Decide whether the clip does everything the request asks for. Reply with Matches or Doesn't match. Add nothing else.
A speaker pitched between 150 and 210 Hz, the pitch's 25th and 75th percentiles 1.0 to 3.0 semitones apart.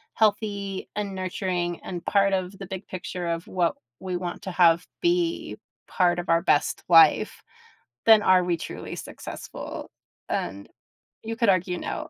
Matches